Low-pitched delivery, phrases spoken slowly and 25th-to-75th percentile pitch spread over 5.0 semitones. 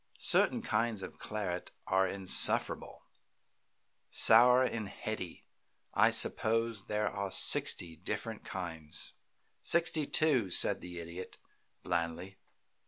No: low, 100 Hz; slow, 100 wpm; average, 4.2 semitones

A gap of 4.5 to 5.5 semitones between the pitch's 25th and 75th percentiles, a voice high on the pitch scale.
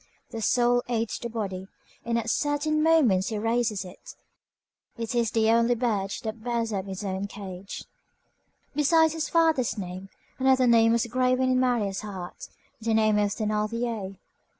No: average, 3.3 semitones; high, 230 Hz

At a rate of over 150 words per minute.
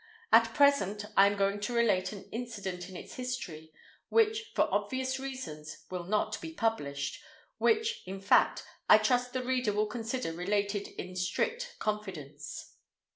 No: average, 145 wpm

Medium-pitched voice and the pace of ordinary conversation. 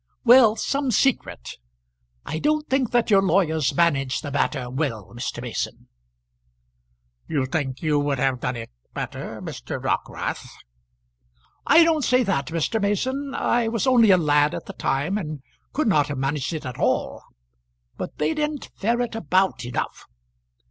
Yes: medium, 170 Hz; average, 155 wpm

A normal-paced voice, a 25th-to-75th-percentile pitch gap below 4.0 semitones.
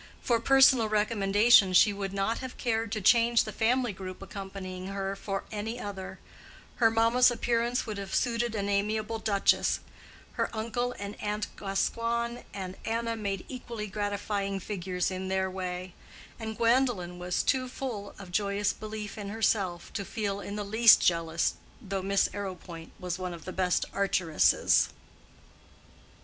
Yes: average, 150 wpm; average, 3.0 semitones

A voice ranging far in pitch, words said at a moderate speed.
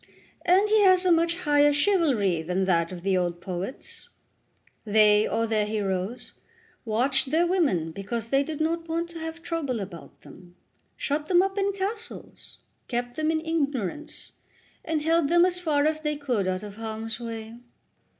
Yes: wide, 7.9 semitones; average, 170 wpm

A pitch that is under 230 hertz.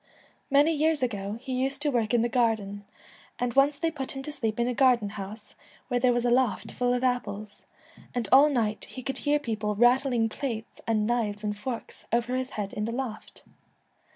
No: high, 240 Hz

